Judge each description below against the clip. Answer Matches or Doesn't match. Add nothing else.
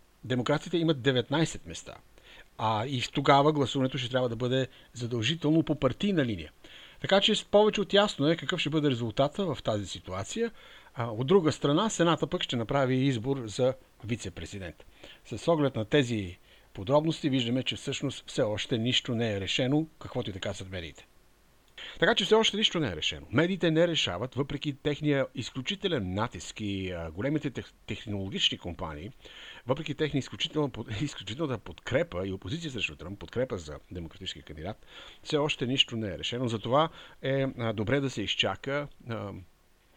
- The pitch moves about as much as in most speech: Doesn't match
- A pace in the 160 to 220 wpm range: Doesn't match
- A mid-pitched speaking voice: Doesn't match